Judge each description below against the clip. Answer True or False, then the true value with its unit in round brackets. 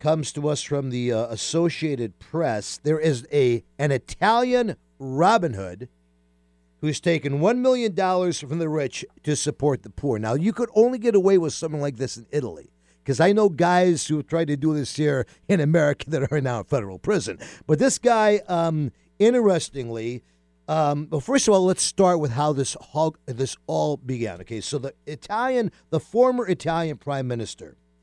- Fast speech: False (180 wpm)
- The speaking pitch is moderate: True (150 Hz)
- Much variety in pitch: True (5.8 semitones)